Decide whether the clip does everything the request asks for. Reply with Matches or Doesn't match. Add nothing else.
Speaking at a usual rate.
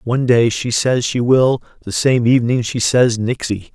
Matches